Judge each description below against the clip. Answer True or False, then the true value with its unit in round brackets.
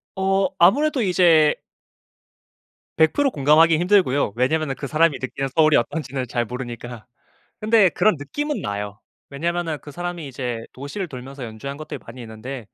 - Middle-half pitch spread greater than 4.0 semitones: True (5.6 semitones)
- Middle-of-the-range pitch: True (150 Hz)